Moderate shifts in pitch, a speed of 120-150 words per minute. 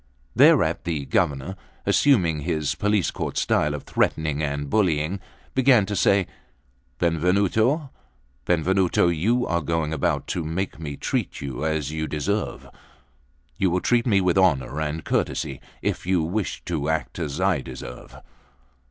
Yes: average, 4.2 semitones; average, 145 wpm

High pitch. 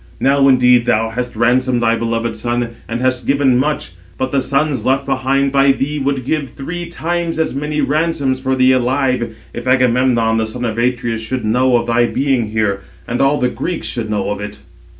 No: low, 130 Hz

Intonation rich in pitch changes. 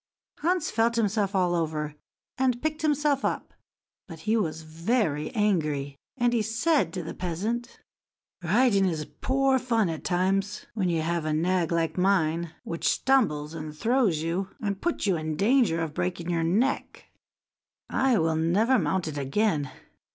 Yes: wide, 6.2 semitones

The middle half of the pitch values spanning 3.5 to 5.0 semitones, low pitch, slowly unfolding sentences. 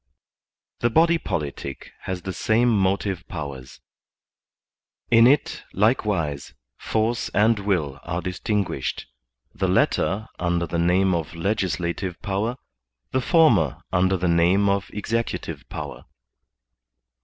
Yes: average, 4.3 semitones; very low, 95 Hz; slow, 110 wpm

